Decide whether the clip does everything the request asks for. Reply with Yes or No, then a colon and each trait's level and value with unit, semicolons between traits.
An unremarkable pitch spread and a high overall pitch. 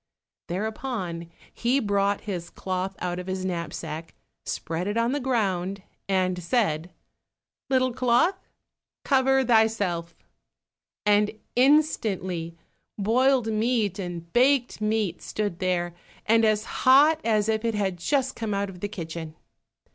Yes: average, 4.9 semitones; high, 205 Hz